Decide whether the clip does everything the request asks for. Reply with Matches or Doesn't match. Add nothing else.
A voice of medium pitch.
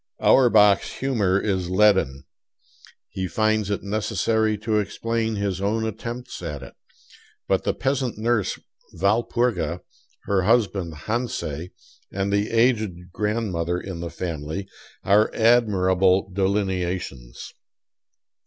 Doesn't match